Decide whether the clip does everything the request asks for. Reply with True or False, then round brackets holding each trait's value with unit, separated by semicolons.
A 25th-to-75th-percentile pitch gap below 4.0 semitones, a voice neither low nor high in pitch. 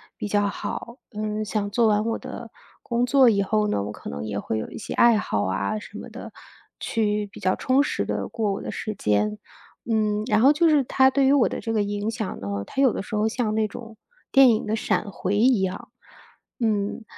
False (2.7 semitones; 215 Hz)